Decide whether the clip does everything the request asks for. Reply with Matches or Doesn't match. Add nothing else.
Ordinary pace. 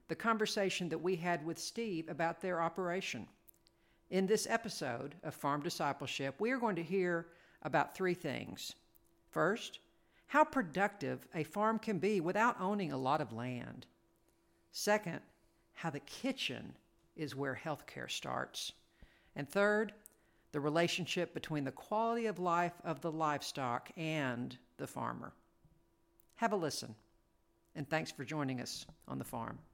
Matches